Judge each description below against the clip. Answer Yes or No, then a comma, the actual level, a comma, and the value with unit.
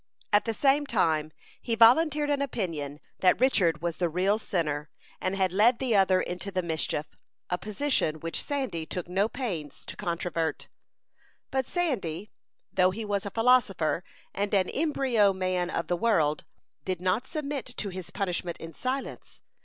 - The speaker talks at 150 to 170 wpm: Yes, average, 160 wpm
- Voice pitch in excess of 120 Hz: Yes, high, 190 Hz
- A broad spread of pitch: Yes, wide, 5.8 semitones